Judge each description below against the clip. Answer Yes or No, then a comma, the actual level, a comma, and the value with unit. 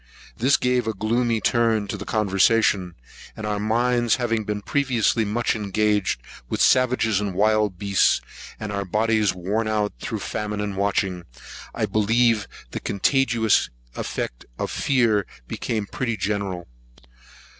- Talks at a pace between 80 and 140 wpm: Yes, slow, 135 wpm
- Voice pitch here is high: No, low, 105 Hz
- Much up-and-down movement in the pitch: No, narrow, 2.4 semitones